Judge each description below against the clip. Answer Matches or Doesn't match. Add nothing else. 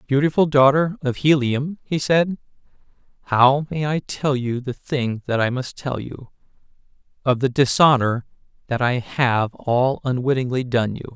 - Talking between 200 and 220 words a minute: Doesn't match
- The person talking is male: Matches